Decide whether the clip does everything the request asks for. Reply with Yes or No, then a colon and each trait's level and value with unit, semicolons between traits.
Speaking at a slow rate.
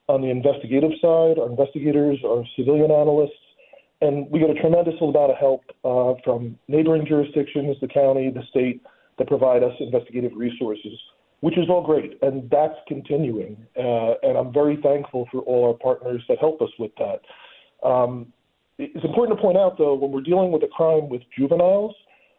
No: average, 175 wpm